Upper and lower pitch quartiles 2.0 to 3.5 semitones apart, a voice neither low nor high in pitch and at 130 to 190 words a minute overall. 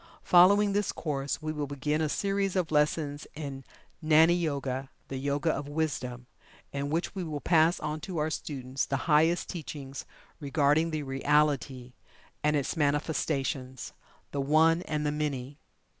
Yes: narrow, 2.5 semitones; medium, 150 Hz; average, 150 wpm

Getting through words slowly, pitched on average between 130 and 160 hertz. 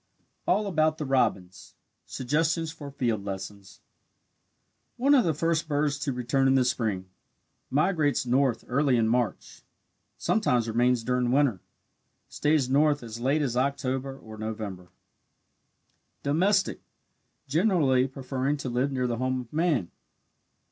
Yes: slow, 130 wpm; low, 135 Hz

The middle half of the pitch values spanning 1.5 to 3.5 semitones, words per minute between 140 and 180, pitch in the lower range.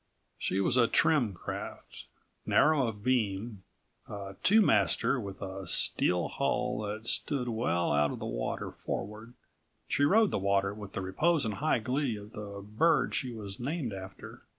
No: average, 4.5 semitones; average, 165 wpm; low, 105 Hz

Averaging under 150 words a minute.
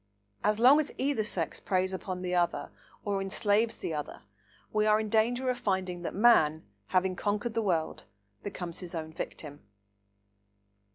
No: average, 160 wpm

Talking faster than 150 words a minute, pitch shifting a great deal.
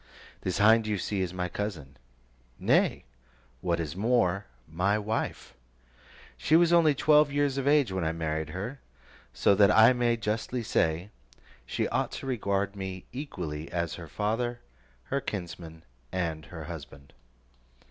No: average, 145 wpm; wide, 6.0 semitones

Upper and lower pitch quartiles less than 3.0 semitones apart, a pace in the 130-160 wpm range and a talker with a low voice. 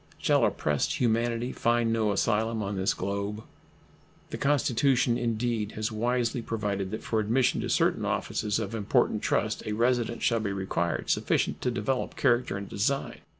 Yes: narrow, 2.6 semitones; average, 155 wpm; low, 115 Hz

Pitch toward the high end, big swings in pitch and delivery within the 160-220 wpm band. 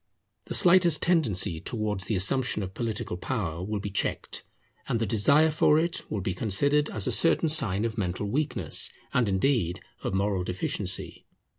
No: low, 105 Hz; wide, 6.9 semitones; average, 165 wpm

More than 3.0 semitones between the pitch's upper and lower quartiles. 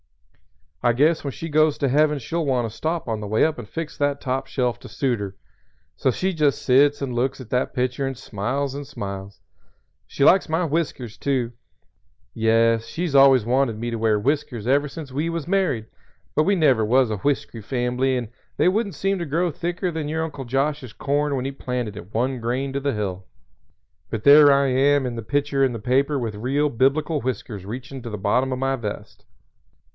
Yes: average, 3.8 semitones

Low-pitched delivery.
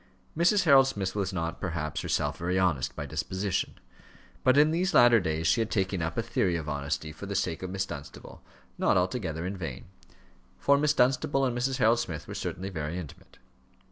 Yes: very low, 95 Hz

